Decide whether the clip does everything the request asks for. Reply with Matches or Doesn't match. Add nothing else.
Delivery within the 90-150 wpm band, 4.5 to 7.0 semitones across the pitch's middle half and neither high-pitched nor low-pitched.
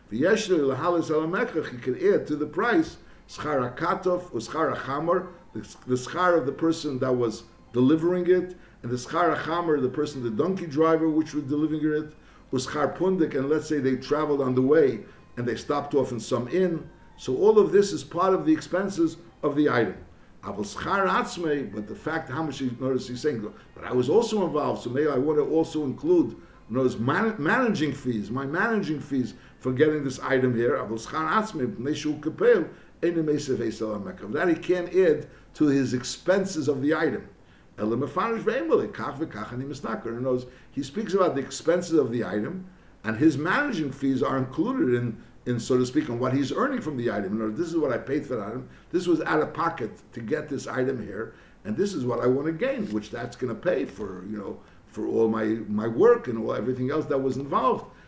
Doesn't match